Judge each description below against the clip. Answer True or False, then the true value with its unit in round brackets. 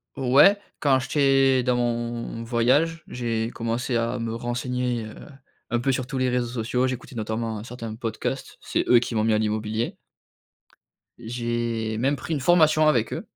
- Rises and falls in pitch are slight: True (2.1 semitones)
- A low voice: True (120 Hz)